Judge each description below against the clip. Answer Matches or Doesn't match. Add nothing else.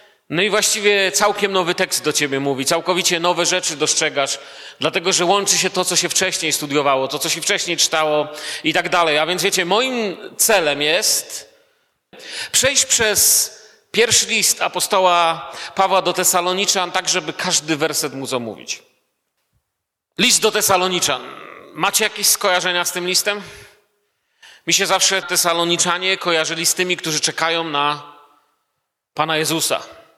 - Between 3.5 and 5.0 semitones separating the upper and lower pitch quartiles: Matches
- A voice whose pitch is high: Doesn't match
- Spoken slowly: Doesn't match